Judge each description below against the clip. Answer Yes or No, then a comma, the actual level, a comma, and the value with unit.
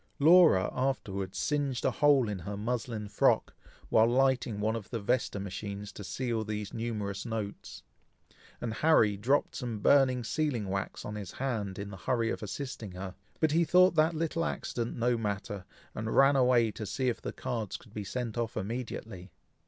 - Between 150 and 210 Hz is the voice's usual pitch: No, low, 115 Hz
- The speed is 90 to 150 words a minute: No, average, 175 wpm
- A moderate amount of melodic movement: Yes, average, 4.2 semitones